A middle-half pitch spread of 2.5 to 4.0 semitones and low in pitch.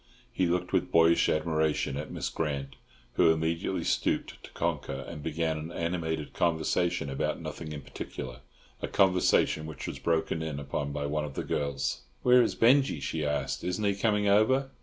Yes: average, 3.3 semitones; very low, 80 Hz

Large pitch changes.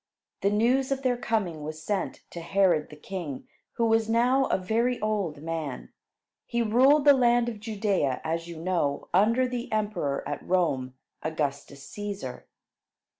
Yes: wide, 6.7 semitones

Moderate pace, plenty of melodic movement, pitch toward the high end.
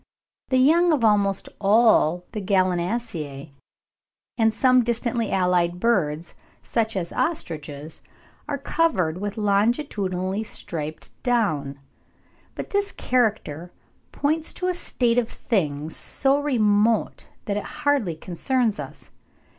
No: slow, 120 wpm; wide, 6.1 semitones; high, 210 Hz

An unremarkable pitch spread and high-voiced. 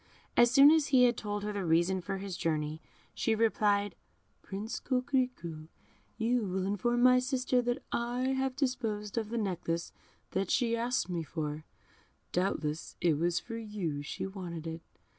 No: wide, 6.0 semitones; high, 210 Hz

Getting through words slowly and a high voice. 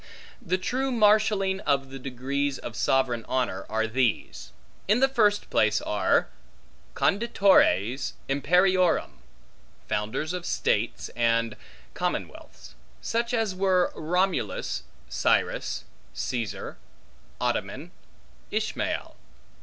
No: slow, 95 wpm; medium, 155 Hz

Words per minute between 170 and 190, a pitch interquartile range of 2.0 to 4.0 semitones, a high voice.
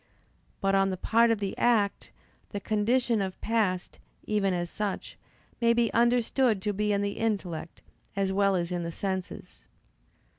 No: average, 160 wpm; average, 3.0 semitones; high, 205 Hz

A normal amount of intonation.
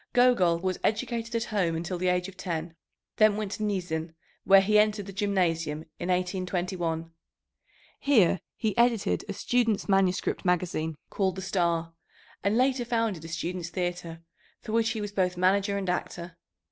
Yes: average, 3.4 semitones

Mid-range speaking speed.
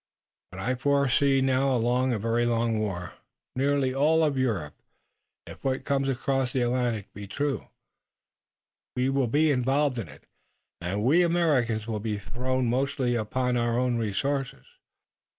Yes: average, 150 wpm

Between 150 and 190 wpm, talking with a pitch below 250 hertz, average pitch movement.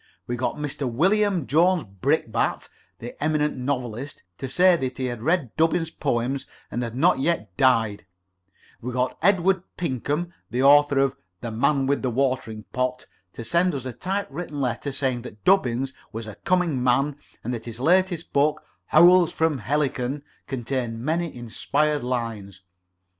Yes: average, 160 wpm; low, 135 Hz; average, 4.6 semitones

